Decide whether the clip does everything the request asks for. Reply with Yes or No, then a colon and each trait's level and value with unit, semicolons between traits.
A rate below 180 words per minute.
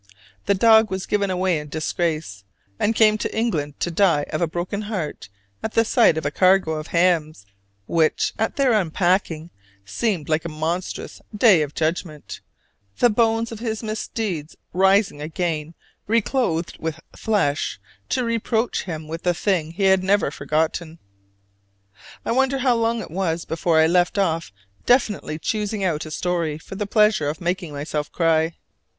Yes: average, 160 wpm